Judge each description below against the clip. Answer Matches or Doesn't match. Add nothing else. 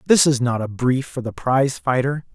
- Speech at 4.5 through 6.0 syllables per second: Matches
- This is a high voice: Doesn't match